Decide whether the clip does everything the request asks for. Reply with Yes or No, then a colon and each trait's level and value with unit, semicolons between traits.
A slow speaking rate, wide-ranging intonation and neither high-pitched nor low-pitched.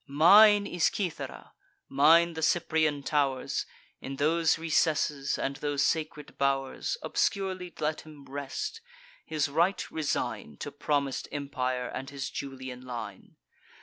No: slow, 120 wpm; average, 2.9 semitones; medium, 145 Hz